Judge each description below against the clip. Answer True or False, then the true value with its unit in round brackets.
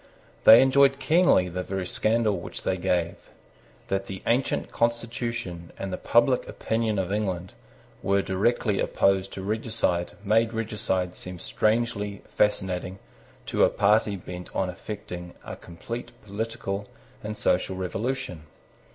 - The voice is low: True (100 Hz)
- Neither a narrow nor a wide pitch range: True (3.8 semitones)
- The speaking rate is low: True (130 wpm)